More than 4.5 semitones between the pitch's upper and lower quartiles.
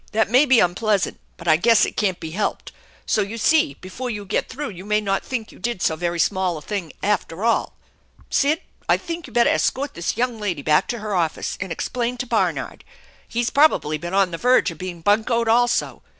Yes: average, 5.0 semitones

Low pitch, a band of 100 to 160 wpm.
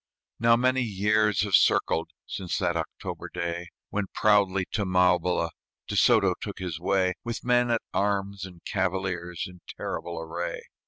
Yes: very low, 95 Hz; average, 150 wpm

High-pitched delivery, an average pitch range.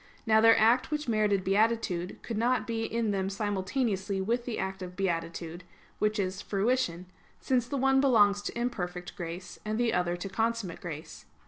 Yes: high, 205 Hz; average, 3.9 semitones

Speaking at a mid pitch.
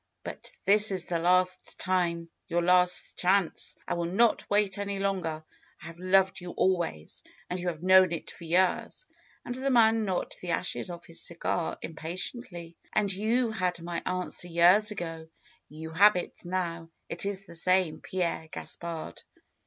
Yes: medium, 180 Hz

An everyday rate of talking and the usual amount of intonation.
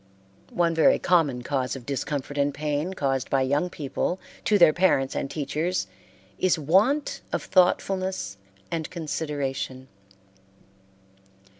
No: slow, 120 wpm; average, 4.6 semitones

